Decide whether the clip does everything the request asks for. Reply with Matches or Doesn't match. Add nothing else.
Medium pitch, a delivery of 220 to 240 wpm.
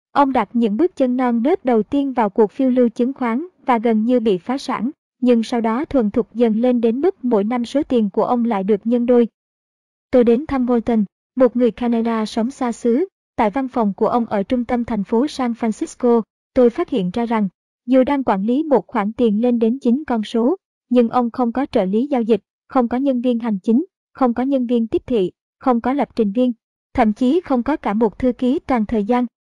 Doesn't match